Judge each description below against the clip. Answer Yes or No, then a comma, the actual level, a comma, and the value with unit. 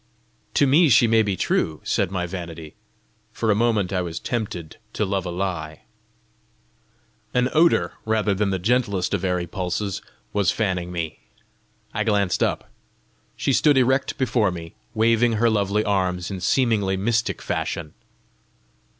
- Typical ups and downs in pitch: Yes, average, 4.1 semitones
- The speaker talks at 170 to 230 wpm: No, average, 150 wpm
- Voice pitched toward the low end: Yes, low, 100 Hz